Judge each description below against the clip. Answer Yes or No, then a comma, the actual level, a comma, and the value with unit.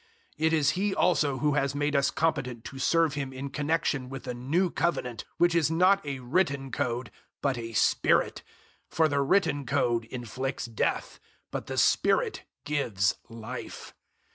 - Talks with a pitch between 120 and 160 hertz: Yes, medium, 140 Hz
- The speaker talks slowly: No, average, 165 wpm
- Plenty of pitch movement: No, average, 4.1 semitones